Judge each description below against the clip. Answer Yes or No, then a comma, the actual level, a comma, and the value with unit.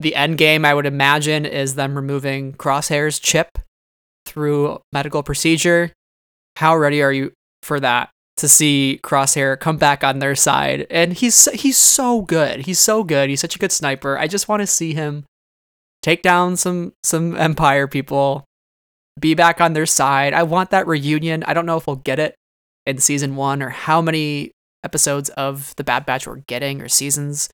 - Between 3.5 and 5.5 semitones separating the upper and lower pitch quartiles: No, average, 2.9 semitones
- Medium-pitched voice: Yes, medium, 145 Hz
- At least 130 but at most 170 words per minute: No, average, 185 wpm